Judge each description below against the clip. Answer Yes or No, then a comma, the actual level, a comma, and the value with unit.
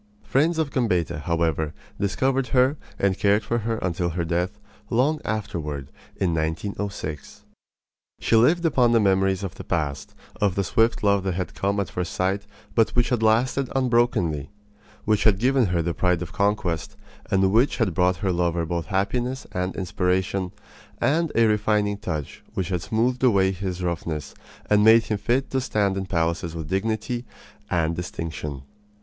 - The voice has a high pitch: No, low, 100 Hz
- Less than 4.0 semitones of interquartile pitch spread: No, average, 4.7 semitones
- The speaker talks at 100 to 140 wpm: No, average, 165 wpm